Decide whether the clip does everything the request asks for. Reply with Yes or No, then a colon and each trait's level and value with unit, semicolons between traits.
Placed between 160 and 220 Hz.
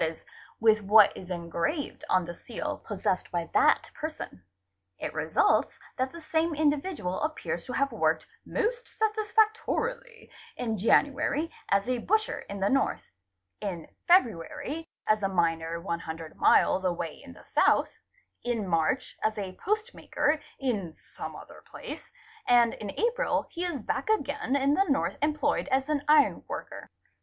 No: very high, 255 Hz